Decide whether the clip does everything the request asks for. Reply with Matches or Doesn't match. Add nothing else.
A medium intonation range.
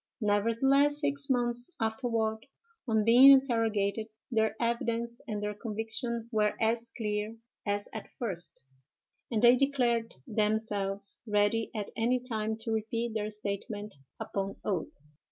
Doesn't match